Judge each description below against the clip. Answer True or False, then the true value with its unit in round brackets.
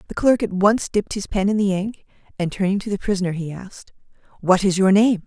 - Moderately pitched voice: False (195 Hz)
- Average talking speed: False (240 wpm)